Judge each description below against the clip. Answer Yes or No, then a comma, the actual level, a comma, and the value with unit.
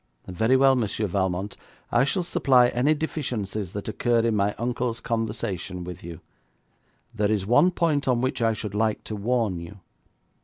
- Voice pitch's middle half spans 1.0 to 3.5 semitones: No, average, 3.9 semitones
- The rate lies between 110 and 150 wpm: No, average, 165 wpm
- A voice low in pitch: Yes, low, 110 Hz